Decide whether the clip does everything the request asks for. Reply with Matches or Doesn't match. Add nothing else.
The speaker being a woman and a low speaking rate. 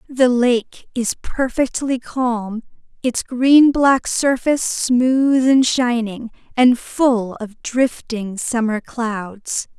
Matches